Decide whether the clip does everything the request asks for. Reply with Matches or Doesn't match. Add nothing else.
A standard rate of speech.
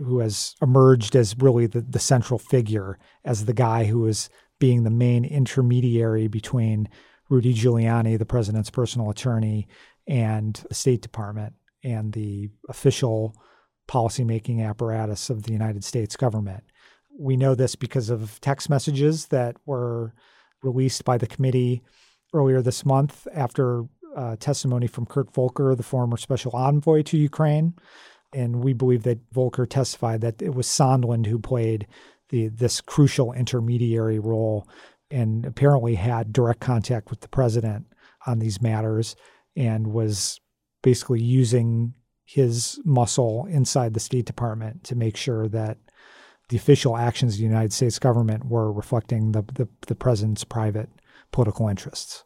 Matches